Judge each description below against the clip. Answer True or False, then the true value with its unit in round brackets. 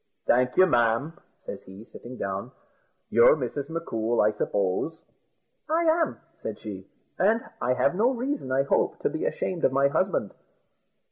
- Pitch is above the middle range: False (140 Hz)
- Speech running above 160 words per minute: False (155 wpm)